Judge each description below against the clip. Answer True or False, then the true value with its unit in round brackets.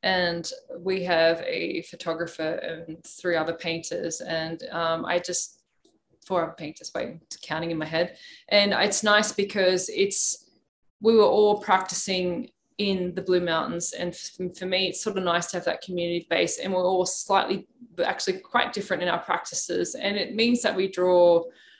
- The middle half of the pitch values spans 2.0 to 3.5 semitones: True (2.8 semitones)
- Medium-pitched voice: True (180 Hz)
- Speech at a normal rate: True (170 wpm)